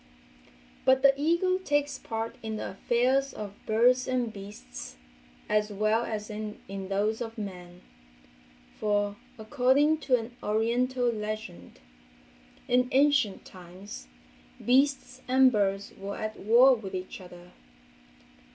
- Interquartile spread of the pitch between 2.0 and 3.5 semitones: No, average, 3.9 semitones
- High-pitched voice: Yes, high, 220 Hz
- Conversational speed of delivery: No, slow, 120 wpm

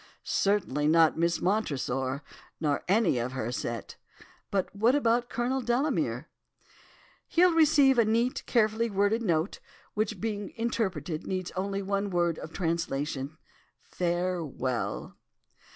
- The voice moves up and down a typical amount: No, wide, 6.3 semitones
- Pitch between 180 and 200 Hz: Yes, high, 190 Hz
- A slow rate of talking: Yes, slow, 120 wpm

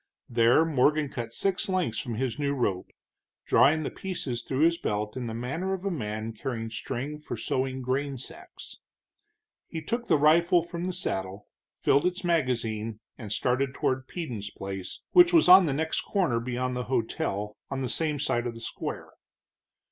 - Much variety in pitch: Yes, wide, 5.9 semitones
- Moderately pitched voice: No, low, 130 Hz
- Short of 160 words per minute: No, average, 175 wpm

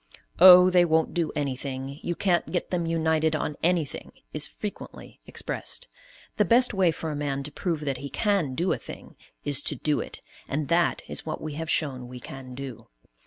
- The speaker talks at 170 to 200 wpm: Yes, average, 195 wpm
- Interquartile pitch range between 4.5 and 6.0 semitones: No, average, 3.9 semitones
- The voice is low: No, medium, 155 Hz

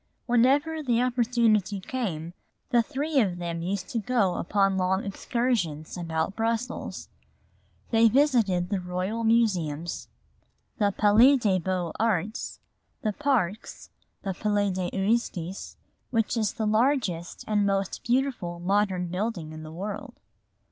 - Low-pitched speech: No, high, 205 Hz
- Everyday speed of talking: No, slow, 125 wpm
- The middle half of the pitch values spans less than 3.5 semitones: No, average, 4.6 semitones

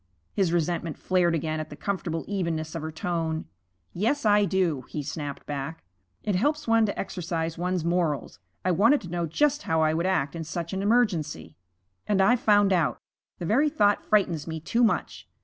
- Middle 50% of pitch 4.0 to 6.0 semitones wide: Yes, average, 4.3 semitones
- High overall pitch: No, medium, 175 Hz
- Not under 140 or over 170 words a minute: No, average, 185 wpm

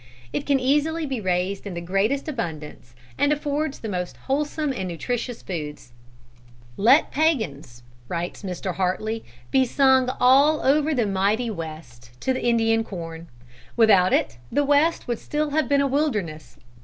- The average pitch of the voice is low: No, high, 225 Hz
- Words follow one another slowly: No, average, 150 wpm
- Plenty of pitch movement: Yes, wide, 7.7 semitones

